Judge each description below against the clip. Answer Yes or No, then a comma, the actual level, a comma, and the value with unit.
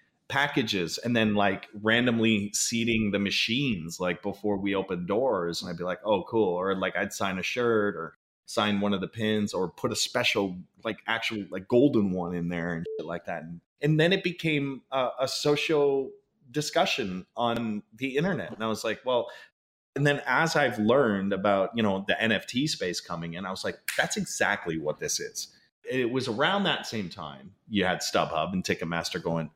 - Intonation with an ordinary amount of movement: No, wide, 6.0 semitones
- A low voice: Yes, low, 110 Hz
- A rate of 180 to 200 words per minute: Yes, average, 195 wpm